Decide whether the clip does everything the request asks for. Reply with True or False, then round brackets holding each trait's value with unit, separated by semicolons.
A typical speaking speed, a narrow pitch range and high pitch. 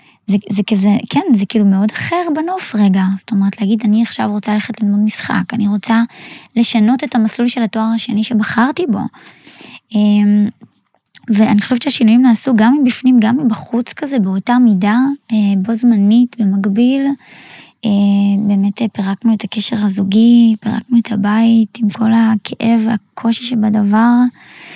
True (135 wpm; 2.3 semitones; 220 Hz)